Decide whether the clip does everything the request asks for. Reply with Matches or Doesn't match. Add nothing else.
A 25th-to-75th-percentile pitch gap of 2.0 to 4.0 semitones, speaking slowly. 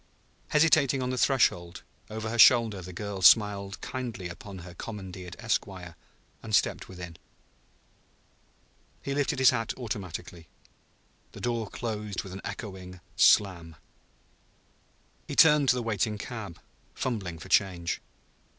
Doesn't match